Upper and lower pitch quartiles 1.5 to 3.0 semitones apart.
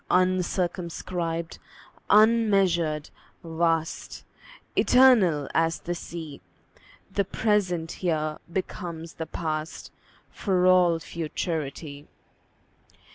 Yes: narrow, 2.4 semitones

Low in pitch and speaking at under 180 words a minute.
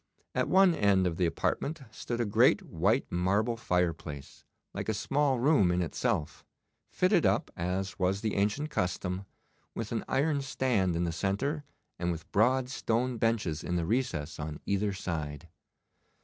Yes: low, 100 Hz; average, 160 wpm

